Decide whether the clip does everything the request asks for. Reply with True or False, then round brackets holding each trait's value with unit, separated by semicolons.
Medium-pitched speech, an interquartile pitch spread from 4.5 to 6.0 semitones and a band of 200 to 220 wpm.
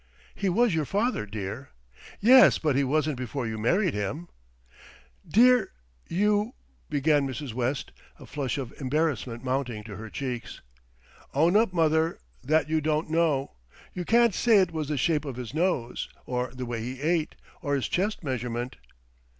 False (145 Hz; 5.3 semitones; 165 wpm)